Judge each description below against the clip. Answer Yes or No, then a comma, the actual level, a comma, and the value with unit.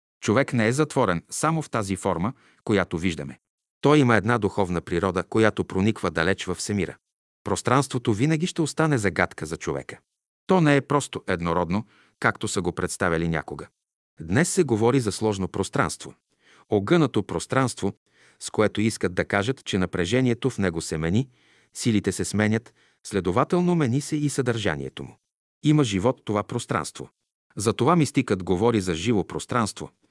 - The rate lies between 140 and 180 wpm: Yes, average, 150 wpm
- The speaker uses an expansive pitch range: Yes, wide, 6.1 semitones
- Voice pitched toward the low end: Yes, low, 110 Hz